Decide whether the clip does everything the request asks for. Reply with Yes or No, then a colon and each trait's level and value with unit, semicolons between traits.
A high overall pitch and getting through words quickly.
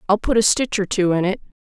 Yes: high, 200 Hz; fast, 295 wpm